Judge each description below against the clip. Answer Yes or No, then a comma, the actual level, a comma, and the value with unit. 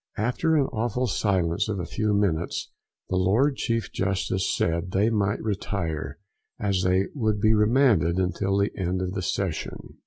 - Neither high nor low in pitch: No, low, 100 Hz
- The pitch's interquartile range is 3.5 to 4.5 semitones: No, average, 3.0 semitones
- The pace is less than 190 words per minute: Yes, average, 160 wpm